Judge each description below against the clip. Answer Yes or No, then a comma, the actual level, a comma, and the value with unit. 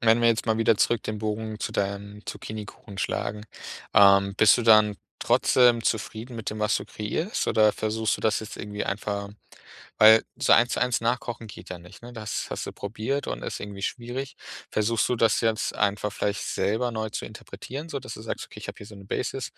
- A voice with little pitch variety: Yes, narrow, 2.0 semitones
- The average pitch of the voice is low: Yes, low, 110 Hz